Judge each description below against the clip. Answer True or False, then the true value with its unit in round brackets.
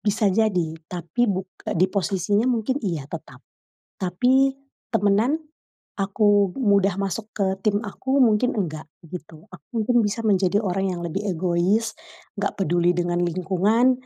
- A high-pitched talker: True (200 Hz)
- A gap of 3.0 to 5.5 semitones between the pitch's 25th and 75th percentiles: True (3.5 semitones)